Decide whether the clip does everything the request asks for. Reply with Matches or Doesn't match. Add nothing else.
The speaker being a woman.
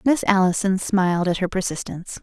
Matches